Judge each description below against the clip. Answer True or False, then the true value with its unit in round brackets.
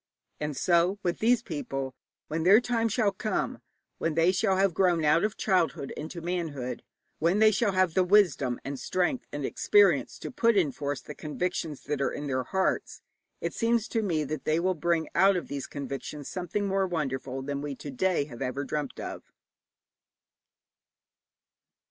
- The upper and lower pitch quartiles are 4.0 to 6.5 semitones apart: True (5.0 semitones)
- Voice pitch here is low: False (170 Hz)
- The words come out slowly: False (175 wpm)